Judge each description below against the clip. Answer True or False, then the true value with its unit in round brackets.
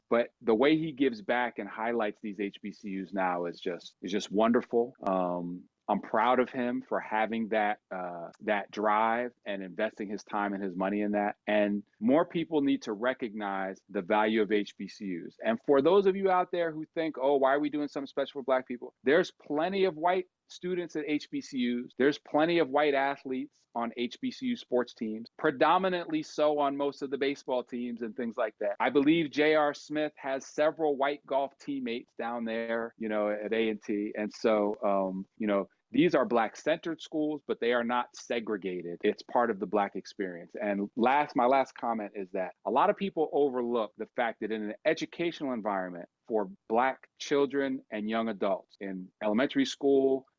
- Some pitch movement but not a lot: False (5.7 semitones)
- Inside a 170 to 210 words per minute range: True (185 wpm)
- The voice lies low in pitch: True (120 Hz)